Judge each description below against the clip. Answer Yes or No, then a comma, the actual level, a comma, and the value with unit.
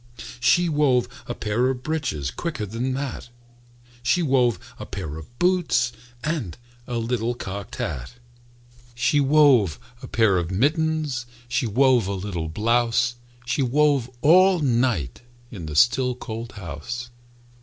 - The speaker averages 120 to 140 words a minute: Yes, slow, 135 wpm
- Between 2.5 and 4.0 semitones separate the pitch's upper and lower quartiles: No, average, 4.8 semitones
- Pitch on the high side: No, low, 120 Hz